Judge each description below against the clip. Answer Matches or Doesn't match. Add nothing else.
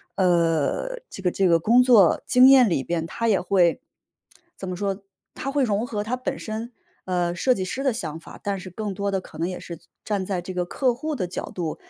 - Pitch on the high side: Matches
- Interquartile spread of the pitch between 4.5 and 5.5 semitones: Matches